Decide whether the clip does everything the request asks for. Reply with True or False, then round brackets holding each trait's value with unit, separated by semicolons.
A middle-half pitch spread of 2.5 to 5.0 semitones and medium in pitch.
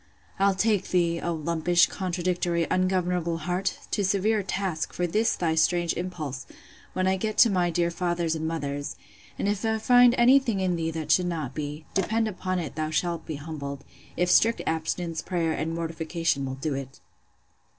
True (2.8 semitones; 175 Hz)